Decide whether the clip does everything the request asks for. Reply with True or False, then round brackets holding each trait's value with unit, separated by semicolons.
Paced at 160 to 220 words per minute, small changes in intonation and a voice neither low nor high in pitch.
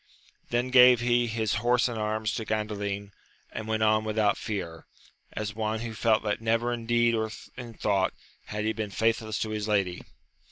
False (185 wpm; 1.6 semitones; 110 Hz)